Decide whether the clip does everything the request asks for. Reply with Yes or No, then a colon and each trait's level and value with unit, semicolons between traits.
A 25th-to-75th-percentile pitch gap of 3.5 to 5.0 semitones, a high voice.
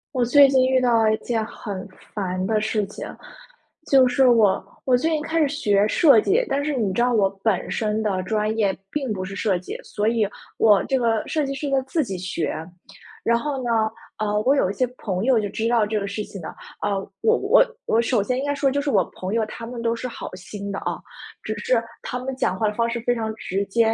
Yes: average, 3.9 semitones; high, 225 Hz